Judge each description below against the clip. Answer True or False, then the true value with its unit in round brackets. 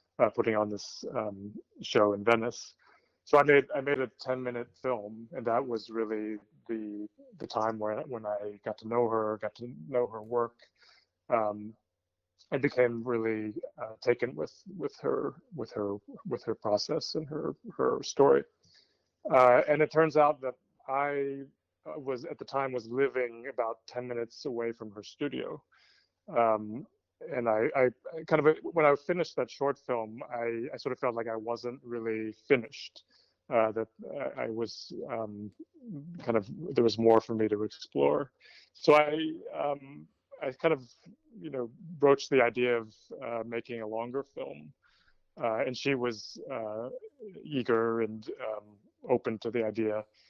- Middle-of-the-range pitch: False (115 Hz)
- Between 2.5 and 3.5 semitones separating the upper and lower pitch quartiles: False (3.9 semitones)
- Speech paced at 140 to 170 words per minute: True (165 wpm)